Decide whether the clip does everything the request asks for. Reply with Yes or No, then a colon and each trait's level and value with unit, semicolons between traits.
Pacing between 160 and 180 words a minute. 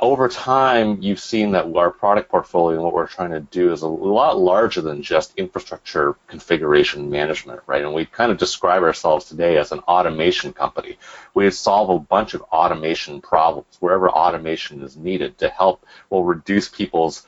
Yes: average, 175 wpm